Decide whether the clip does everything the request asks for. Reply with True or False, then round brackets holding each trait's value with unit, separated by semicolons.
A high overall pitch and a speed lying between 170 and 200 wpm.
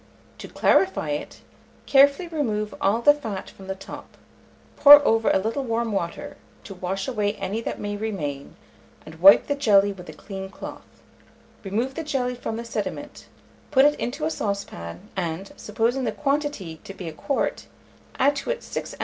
True (215 Hz; 175 wpm)